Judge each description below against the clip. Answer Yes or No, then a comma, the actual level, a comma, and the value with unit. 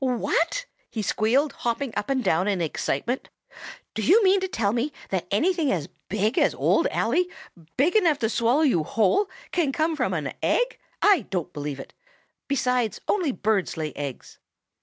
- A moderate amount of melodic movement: No, wide, 7.8 semitones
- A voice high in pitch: Yes, high, 245 Hz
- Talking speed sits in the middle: Yes, average, 170 wpm